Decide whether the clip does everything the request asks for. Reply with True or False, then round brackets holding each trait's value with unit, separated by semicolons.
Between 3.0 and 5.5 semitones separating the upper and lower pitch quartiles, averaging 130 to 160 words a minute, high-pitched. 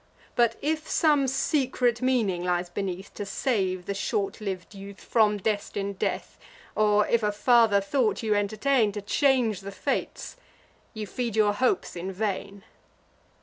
True (3.5 semitones; 145 wpm; 210 Hz)